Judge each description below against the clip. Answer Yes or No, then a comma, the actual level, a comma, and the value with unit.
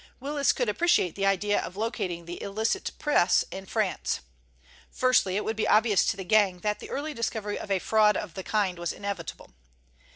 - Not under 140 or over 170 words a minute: No, average, 190 wpm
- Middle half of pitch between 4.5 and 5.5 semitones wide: No, average, 2.9 semitones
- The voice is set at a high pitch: Yes, high, 205 Hz